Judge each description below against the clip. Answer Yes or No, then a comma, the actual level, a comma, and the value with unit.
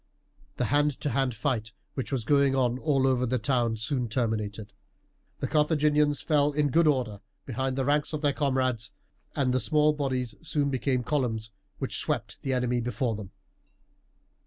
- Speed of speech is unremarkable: Yes, average, 175 wpm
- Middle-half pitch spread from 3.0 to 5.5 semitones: Yes, average, 3.3 semitones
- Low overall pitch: Yes, low, 130 Hz